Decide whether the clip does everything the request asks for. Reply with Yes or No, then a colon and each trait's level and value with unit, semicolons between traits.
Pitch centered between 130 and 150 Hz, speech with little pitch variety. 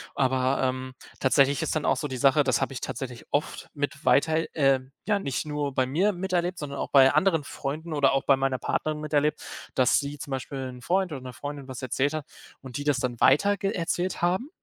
No: medium, 140 Hz; average, 3.0 semitones